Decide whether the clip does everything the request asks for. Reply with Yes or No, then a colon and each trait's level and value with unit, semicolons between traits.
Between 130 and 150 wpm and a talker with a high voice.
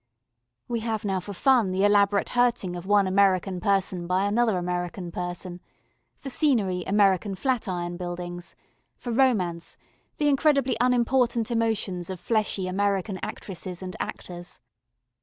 Yes: slow, 135 wpm; high, 195 Hz